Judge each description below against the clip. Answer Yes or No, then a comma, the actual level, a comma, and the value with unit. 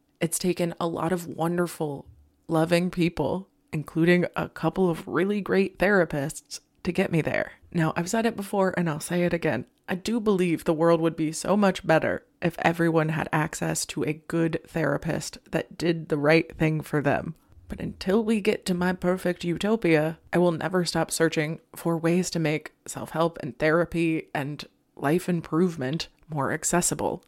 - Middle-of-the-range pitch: Yes, medium, 165 Hz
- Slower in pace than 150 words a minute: No, average, 175 wpm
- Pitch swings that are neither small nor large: No, narrow, 2.2 semitones